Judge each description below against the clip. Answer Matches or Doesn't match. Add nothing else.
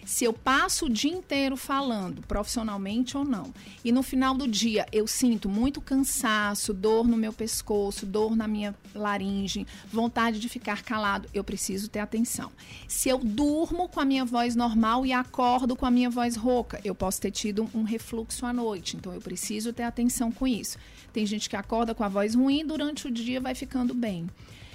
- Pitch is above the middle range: Matches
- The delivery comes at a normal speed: Doesn't match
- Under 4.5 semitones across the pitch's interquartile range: Matches